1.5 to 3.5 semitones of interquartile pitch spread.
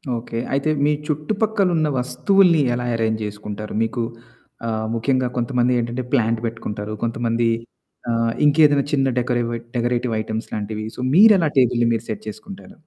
No: average, 4.2 semitones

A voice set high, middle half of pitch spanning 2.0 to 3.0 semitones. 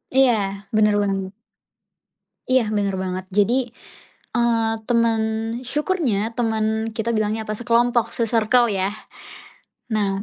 Yes: high, 220 Hz; narrow, 2.4 semitones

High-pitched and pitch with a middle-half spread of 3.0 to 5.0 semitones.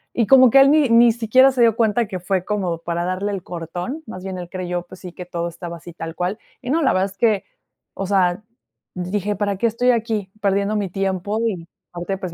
Yes: high, 195 Hz; average, 3.9 semitones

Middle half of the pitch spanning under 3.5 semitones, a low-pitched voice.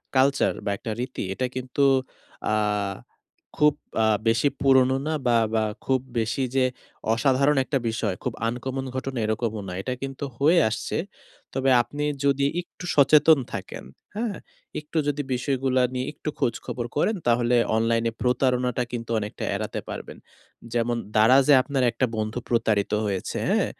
Yes: average, 2.9 semitones; low, 130 Hz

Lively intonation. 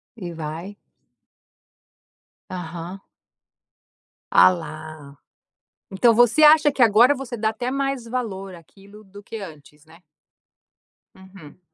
Yes: wide, 6.2 semitones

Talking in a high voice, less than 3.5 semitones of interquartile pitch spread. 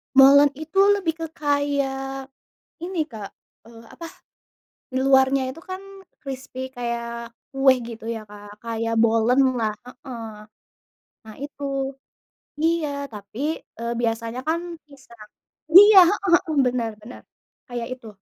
No: very high, 265 Hz; average, 3.8 semitones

